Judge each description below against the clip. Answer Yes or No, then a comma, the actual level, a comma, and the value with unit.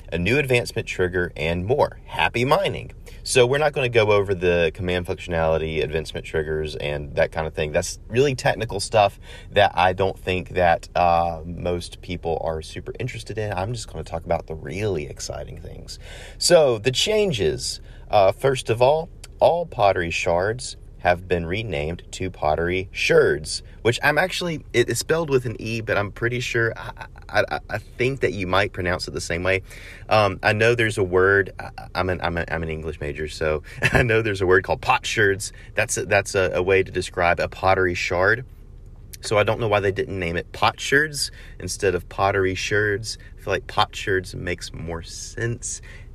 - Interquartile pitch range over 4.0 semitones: Yes, average, 4.5 semitones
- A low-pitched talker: Yes, very low, 95 Hz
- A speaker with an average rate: Yes, average, 195 wpm